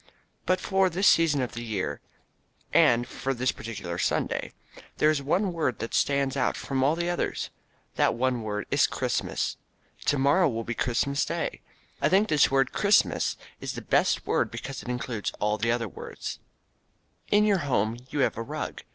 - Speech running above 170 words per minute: Yes, average, 185 wpm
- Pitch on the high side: No, low, 135 Hz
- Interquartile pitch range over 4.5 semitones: Yes, wide, 5.5 semitones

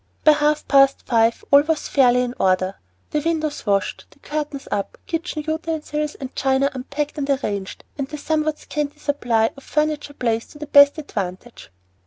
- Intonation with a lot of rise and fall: No, average, 3.7 semitones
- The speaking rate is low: No, average, 170 wpm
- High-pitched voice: Yes, very high, 285 Hz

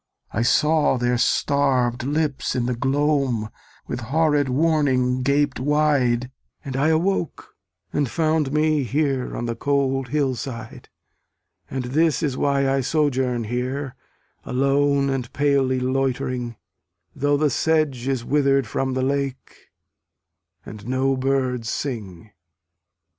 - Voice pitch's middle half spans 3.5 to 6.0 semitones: No, narrow, 2.4 semitones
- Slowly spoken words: Yes, slow, 125 wpm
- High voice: No, low, 135 Hz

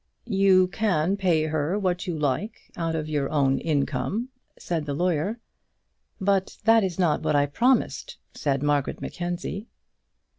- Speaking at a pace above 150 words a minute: No, average, 145 wpm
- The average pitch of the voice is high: No, medium, 175 Hz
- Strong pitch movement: No, average, 4.8 semitones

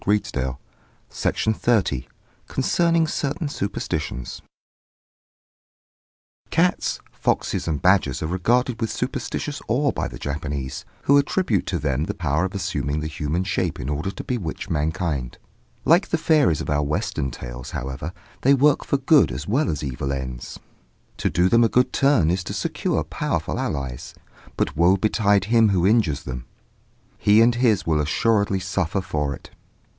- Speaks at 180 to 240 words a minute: No, average, 155 wpm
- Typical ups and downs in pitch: No, wide, 8.0 semitones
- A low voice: Yes, very low, 90 Hz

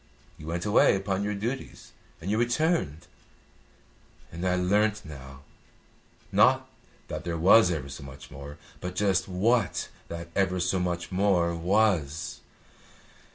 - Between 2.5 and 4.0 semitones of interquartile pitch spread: Yes, average, 3.6 semitones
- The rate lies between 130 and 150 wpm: Yes, slow, 135 wpm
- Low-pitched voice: Yes, very low, 90 Hz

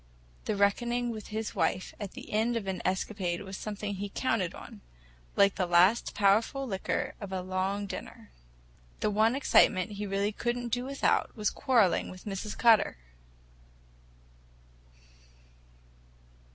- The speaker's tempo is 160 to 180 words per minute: No, average, 140 wpm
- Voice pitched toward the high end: Yes, high, 205 Hz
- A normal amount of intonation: Yes, average, 3.1 semitones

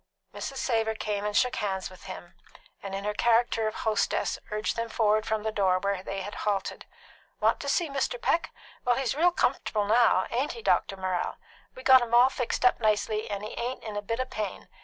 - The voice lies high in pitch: Yes, high, 220 Hz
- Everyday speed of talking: No, fast, 215 wpm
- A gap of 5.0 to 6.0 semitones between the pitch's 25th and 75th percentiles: No, average, 3.1 semitones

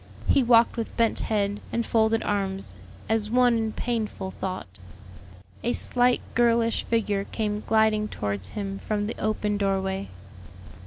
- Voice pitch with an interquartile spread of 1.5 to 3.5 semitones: Yes, narrow, 2.5 semitones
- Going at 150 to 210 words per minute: No, average, 140 wpm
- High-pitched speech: Yes, high, 215 Hz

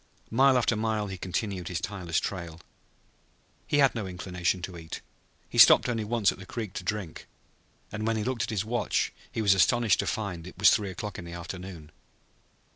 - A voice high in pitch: No, low, 100 Hz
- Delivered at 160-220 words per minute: Yes, average, 200 wpm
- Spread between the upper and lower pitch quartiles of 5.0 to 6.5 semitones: No, average, 3.7 semitones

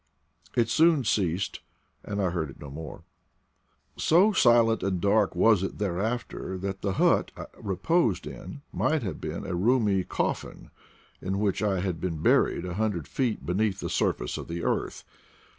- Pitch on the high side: No, low, 100 Hz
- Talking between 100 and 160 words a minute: No, average, 170 wpm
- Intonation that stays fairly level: No, average, 4.0 semitones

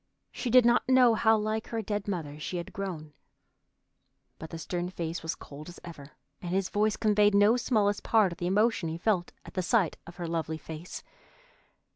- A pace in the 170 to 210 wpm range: Yes, average, 190 wpm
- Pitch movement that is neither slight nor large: Yes, average, 4.5 semitones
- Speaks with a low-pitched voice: No, high, 190 Hz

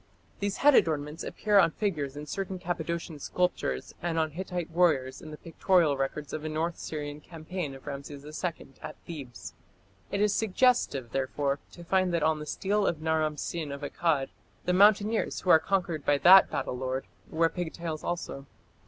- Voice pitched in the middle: Yes, medium, 160 Hz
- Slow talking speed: No, average, 175 wpm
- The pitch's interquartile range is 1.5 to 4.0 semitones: Yes, average, 3.7 semitones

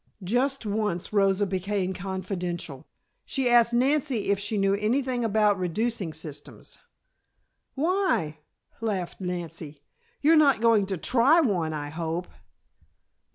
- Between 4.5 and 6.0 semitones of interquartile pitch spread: Yes, average, 5.2 semitones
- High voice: Yes, high, 200 Hz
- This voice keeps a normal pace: No, slow, 120 wpm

